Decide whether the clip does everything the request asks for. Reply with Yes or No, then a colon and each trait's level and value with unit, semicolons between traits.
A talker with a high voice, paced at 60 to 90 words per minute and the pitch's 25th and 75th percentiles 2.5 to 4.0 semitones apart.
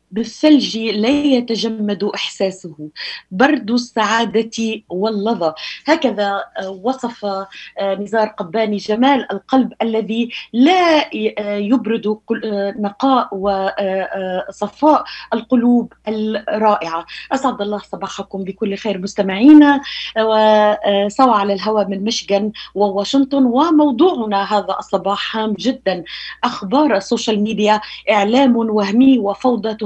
Yes: high, 215 Hz; average, 85 wpm; average, 3.4 semitones